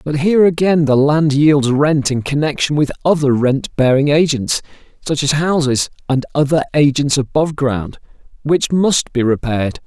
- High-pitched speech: No, medium, 145 Hz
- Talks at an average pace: Yes, average, 160 wpm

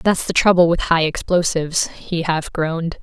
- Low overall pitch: No, medium, 170 Hz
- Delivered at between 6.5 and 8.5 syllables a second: No, 4.9 syllables/s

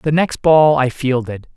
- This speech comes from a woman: No, male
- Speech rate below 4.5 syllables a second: Yes, 4.1 syllables/s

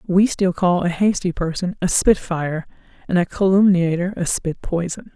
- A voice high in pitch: No, medium, 180 Hz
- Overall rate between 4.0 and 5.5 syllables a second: Yes, 4.8 syllables/s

